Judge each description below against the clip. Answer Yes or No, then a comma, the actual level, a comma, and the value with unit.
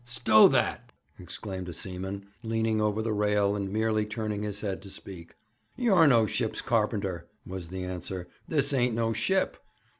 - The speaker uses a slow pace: No, average, 160 wpm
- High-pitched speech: No, low, 105 Hz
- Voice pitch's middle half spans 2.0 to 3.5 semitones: Yes, average, 2.8 semitones